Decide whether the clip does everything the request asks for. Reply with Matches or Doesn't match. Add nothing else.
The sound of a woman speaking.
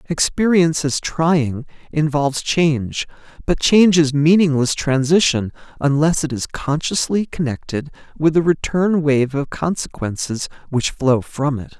Doesn't match